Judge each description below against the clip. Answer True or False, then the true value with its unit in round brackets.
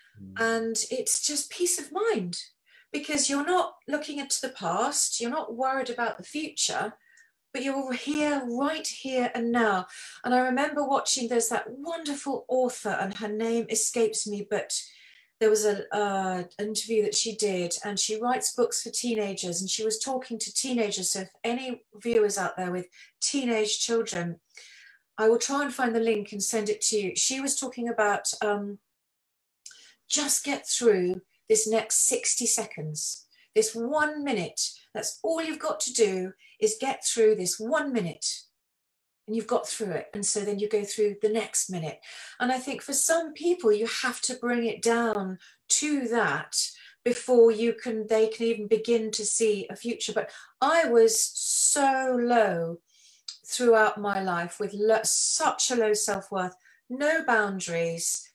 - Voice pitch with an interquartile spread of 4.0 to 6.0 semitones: True (4.7 semitones)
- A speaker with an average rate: True (170 wpm)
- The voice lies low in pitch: False (230 Hz)